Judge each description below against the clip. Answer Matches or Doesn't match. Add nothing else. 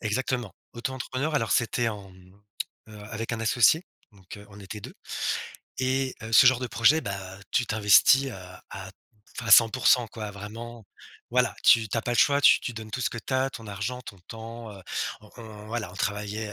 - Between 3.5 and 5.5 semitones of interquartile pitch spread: Doesn't match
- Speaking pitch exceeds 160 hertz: Doesn't match